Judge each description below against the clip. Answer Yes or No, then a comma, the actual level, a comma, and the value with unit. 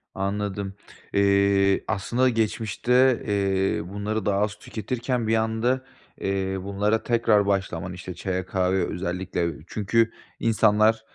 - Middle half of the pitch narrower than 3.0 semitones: Yes, narrow, 2.5 semitones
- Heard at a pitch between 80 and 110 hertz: Yes, low, 100 Hz